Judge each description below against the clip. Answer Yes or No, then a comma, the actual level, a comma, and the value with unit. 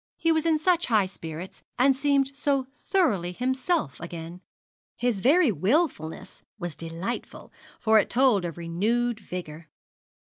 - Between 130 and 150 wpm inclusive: Yes, slow, 135 wpm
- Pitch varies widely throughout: Yes, wide, 8.2 semitones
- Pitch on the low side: No, high, 220 Hz